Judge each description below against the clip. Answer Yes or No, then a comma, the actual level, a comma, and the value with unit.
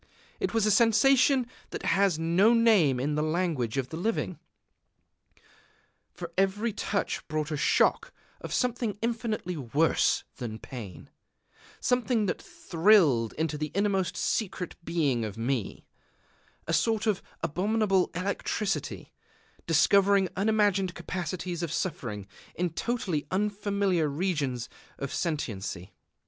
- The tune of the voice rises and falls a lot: Yes, wide, 5.8 semitones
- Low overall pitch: No, medium, 180 Hz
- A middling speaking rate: No, slow, 120 wpm